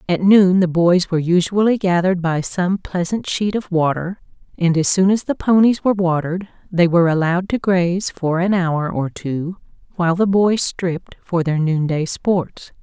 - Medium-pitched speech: Yes, medium, 180 Hz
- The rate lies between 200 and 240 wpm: No, average, 180 wpm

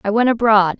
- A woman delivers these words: Yes, female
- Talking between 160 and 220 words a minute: No, fast, 230 wpm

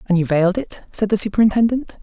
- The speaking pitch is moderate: No, high, 205 Hz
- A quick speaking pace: Yes, fast, 210 wpm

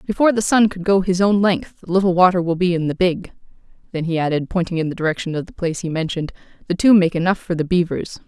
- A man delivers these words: No, female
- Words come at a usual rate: No, fast, 255 wpm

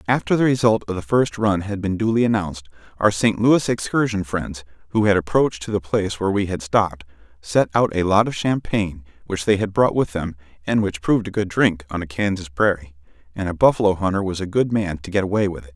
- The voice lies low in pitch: Yes, low, 100 Hz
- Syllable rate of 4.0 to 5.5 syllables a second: No, 6.0 syllables/s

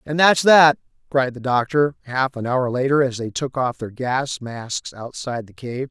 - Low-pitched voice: Yes, low, 130 Hz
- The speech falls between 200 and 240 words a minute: Yes, fast, 205 wpm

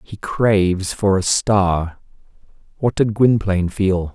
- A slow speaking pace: Yes, slow, 130 wpm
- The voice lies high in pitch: No, low, 100 Hz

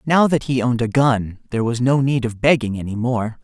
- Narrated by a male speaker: Yes, male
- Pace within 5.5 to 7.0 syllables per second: Yes, 5.6 syllables/s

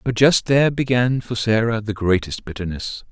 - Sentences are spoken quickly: No, average, 175 wpm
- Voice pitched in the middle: No, low, 115 Hz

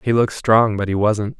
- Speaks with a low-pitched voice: Yes, low, 110 Hz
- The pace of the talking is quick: Yes, fast, 260 wpm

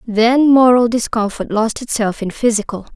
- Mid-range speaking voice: No, high, 230 Hz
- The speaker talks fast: No, average, 140 wpm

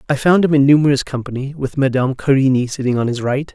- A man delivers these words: Yes, male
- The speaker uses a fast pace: Yes, fast, 220 wpm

